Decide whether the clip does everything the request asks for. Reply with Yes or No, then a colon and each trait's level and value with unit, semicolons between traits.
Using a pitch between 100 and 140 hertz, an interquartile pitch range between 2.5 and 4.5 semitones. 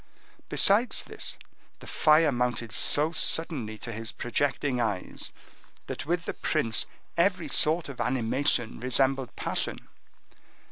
No: low, 135 Hz; average, 5.0 semitones